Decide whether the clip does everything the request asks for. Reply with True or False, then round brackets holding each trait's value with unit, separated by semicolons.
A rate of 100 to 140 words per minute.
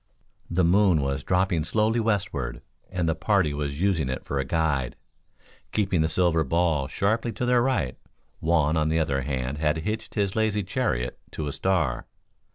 False (170 wpm)